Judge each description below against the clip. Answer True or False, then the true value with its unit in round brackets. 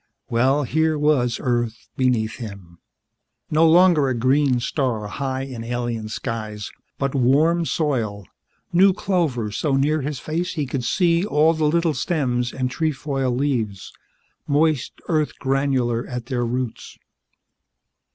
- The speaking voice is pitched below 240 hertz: True (135 Hz)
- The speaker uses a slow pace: True (130 wpm)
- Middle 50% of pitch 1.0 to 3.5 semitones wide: False (4.3 semitones)